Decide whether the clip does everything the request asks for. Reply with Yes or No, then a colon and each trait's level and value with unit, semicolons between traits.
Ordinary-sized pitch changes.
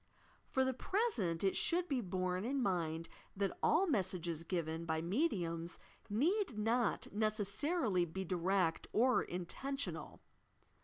No: wide, 7.2 semitones